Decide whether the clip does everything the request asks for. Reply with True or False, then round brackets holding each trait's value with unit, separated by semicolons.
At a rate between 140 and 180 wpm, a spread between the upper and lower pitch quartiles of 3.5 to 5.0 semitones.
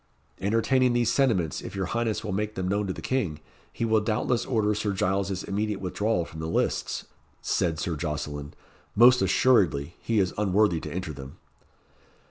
True (170 wpm; 4.2 semitones)